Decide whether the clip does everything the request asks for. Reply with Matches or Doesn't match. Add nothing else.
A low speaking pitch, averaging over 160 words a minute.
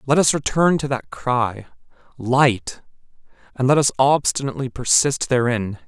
Doesn't match